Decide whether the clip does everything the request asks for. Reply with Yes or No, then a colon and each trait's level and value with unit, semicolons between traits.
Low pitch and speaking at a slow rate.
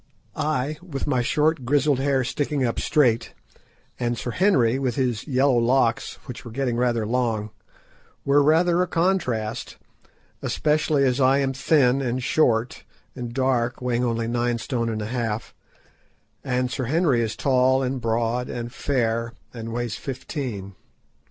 No: low, 125 Hz; average, 150 wpm